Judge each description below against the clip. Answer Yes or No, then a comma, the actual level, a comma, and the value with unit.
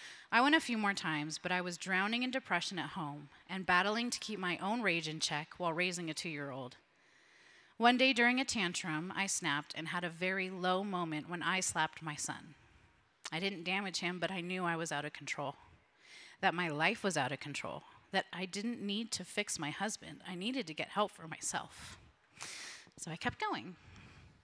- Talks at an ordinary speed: No, fast, 210 wpm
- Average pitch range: Yes, average, 4.2 semitones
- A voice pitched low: No, medium, 180 Hz